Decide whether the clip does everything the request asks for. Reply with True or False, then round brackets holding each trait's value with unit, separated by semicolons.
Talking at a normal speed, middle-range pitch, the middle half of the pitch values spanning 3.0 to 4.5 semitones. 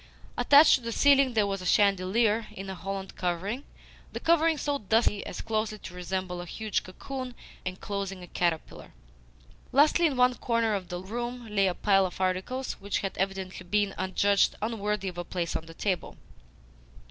False (175 wpm; 200 Hz; 4.1 semitones)